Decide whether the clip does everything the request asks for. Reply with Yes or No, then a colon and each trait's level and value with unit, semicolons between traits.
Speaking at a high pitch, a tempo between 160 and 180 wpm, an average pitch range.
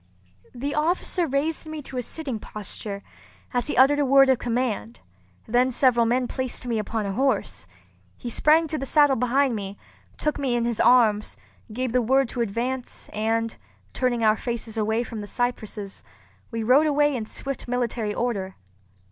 Yes: high, 245 Hz; average, 175 wpm; average, 3.5 semitones